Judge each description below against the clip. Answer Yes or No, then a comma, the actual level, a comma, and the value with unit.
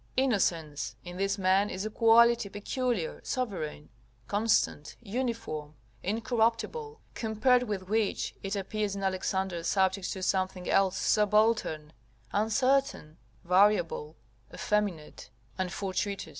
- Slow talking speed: Yes, slow, 105 wpm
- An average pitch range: Yes, average, 3.5 semitones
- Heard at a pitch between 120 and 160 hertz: No, high, 200 Hz